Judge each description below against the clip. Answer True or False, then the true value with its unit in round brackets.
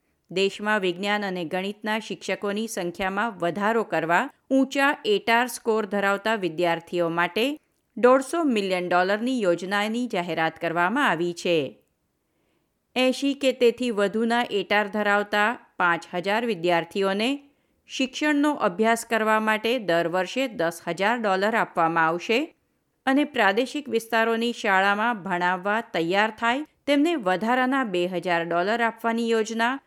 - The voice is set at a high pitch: True (215 Hz)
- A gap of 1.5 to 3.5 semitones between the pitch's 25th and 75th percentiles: False (4.7 semitones)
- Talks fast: False (115 wpm)